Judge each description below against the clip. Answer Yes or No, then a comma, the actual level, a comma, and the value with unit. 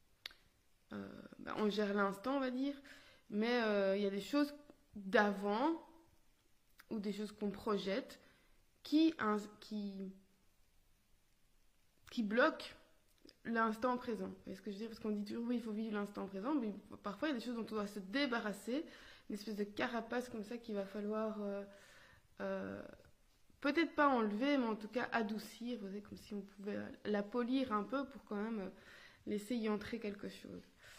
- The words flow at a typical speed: Yes, average, 185 wpm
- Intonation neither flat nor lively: Yes, average, 3.4 semitones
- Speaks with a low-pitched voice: No, high, 215 Hz